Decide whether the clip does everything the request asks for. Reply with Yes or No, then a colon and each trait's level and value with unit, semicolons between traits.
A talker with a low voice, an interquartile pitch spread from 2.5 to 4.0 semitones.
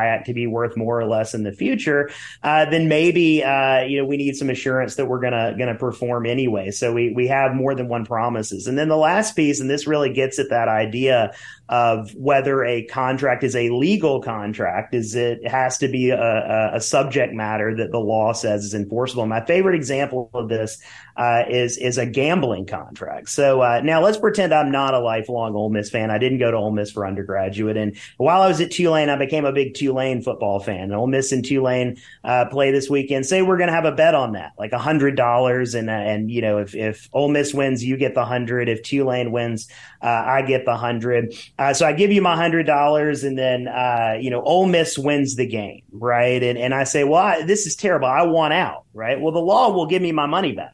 Yes: low, 125 Hz; average, 3.5 semitones